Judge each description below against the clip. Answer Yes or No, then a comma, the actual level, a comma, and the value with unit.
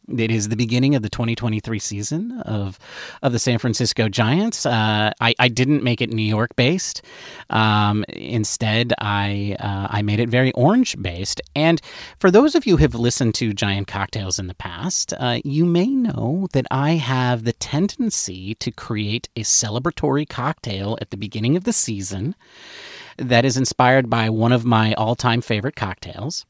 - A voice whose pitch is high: No, low, 120 Hz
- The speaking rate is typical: Yes, average, 175 wpm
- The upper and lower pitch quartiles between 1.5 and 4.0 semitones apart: No, average, 4.8 semitones